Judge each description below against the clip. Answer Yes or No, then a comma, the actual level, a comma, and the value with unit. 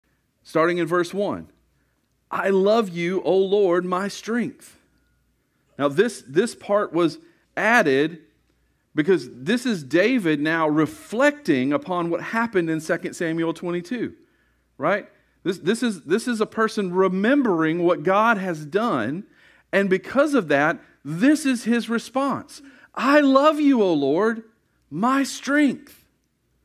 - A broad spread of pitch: Yes, wide, 7.0 semitones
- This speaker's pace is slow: Yes, slow, 130 wpm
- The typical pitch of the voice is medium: No, high, 205 Hz